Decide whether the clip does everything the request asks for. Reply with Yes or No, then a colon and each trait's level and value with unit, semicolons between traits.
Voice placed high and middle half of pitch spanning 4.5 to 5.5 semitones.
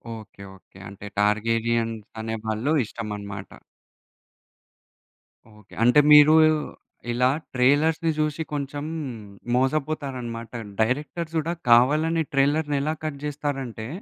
No: low, 130 Hz; average, 4.8 semitones